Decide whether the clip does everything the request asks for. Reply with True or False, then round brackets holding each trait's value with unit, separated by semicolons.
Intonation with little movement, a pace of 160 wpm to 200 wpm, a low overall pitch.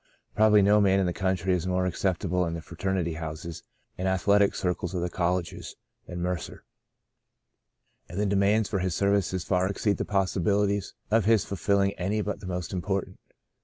True (2.1 semitones; 170 wpm; 95 Hz)